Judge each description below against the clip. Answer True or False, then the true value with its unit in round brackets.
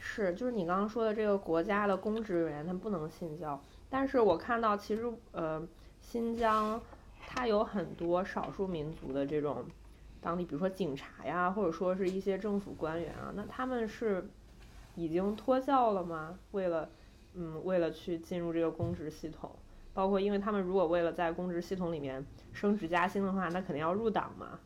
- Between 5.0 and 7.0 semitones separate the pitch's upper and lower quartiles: False (4.2 semitones)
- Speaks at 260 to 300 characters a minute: True (280 characters per minute)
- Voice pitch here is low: False (185 Hz)